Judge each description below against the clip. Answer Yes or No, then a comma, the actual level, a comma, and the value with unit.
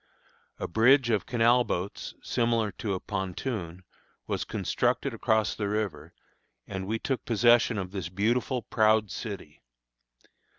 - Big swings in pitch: No, average, 3.6 semitones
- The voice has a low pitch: Yes, low, 110 Hz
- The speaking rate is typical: No, slow, 130 wpm